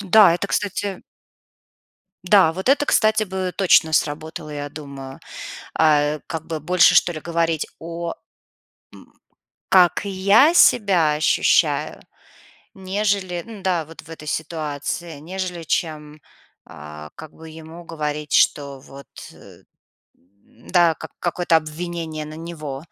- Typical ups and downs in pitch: Yes, average, 3.3 semitones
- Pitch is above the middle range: No, medium, 165 Hz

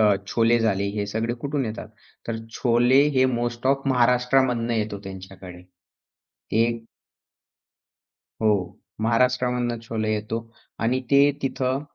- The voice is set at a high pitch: No, low, 120 Hz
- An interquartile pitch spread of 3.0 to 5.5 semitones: No, narrow, 2.5 semitones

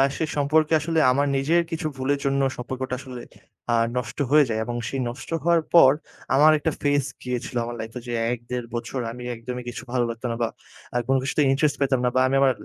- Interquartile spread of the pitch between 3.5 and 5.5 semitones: No, average, 2.7 semitones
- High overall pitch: No, low, 130 Hz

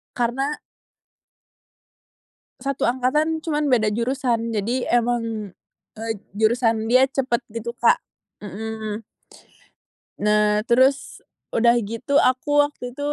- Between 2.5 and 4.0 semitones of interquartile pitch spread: Yes, average, 3.4 semitones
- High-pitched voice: Yes, high, 240 Hz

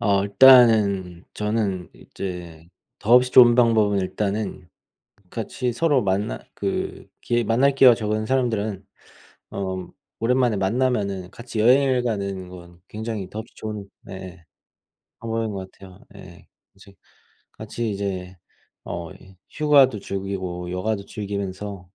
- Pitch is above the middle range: No, low, 105 Hz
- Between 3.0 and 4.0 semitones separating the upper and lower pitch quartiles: Yes, average, 3.7 semitones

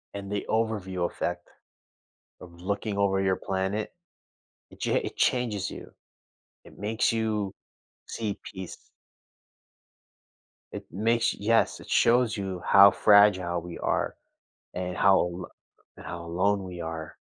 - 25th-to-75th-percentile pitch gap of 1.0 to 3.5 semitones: Yes, average, 2.8 semitones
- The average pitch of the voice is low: Yes, low, 100 Hz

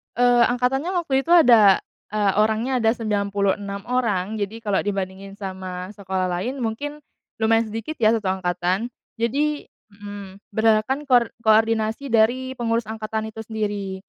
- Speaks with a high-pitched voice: Yes, high, 220 Hz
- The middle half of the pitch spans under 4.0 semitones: Yes, average, 3.3 semitones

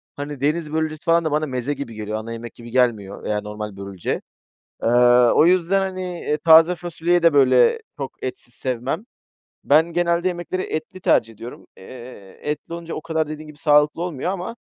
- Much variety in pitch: Yes, wide, 6.0 semitones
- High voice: No, medium, 150 Hz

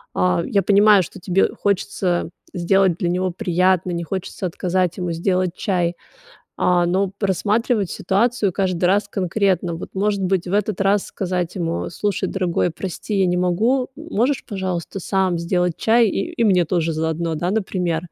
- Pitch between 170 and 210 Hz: Yes, medium, 185 Hz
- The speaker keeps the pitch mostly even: Yes, narrow, 2.3 semitones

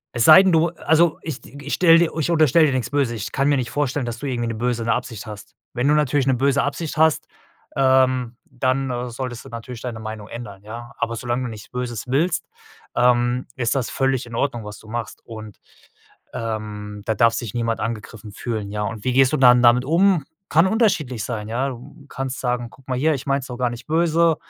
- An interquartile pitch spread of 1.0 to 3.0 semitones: No, average, 3.4 semitones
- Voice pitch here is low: Yes, low, 125 Hz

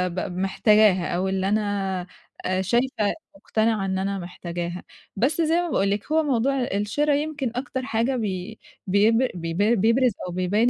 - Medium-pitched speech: No, high, 210 Hz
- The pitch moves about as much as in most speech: Yes, average, 4.9 semitones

